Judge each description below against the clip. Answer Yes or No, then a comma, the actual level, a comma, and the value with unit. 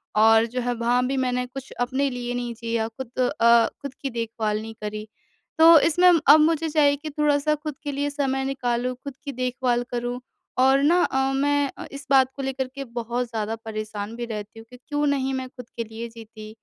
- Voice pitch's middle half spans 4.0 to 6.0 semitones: No, average, 3.2 semitones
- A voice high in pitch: Yes, very high, 250 Hz